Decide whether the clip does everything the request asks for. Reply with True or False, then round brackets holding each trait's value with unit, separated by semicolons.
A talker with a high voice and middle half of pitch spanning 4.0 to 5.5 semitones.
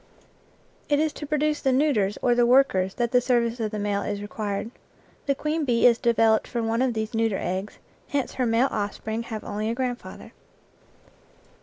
False (235 Hz; 3.2 semitones)